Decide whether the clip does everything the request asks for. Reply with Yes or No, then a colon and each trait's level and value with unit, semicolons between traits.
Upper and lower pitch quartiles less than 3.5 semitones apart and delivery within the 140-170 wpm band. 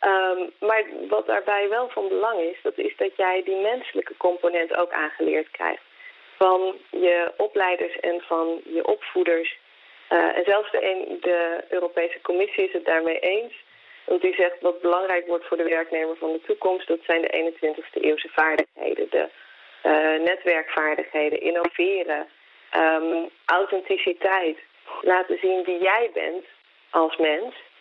Yes: average, 2.9 semitones; average, 145 wpm